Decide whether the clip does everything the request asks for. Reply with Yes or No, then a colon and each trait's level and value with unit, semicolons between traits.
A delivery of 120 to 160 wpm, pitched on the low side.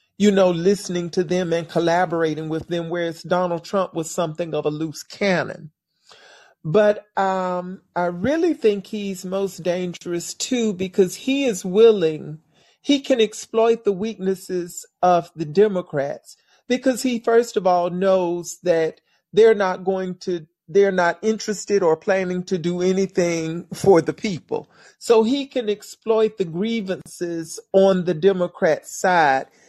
No: average, 145 wpm; medium, 185 Hz